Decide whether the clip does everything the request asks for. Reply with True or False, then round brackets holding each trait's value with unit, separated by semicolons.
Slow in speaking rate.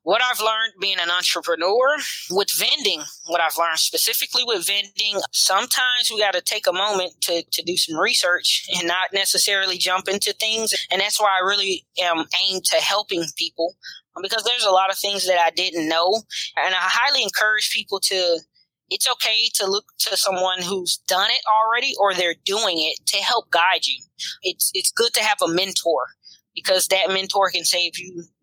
False (185 wpm)